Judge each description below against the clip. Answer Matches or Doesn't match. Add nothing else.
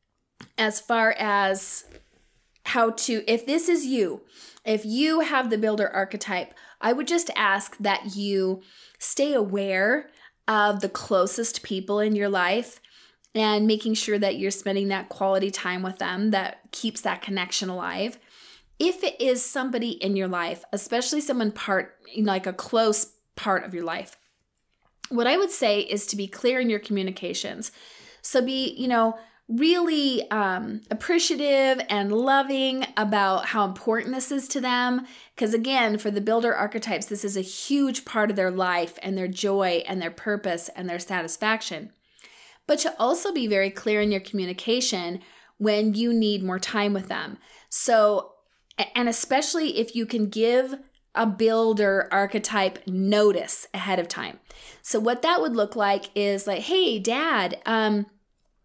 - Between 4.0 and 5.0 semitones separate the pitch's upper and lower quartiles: Doesn't match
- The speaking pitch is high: Matches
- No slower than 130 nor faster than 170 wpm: Matches